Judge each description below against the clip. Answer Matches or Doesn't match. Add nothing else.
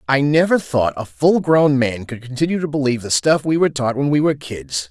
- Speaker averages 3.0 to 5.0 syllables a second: Doesn't match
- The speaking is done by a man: Matches